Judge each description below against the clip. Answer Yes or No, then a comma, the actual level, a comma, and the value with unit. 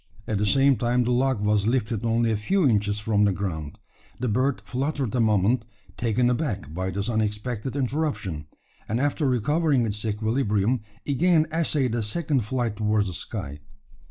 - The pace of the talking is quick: No, average, 165 wpm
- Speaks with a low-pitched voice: Yes, low, 115 Hz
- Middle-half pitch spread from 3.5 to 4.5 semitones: Yes, average, 4.1 semitones